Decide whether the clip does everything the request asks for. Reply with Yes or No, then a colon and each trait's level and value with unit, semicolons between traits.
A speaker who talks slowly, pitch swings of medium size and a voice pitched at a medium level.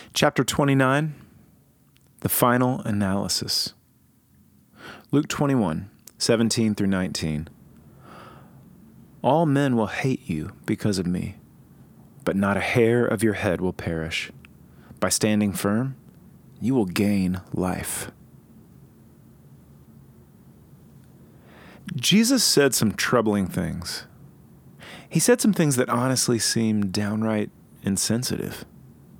No: slow, 105 wpm; average, 5.0 semitones; low, 110 Hz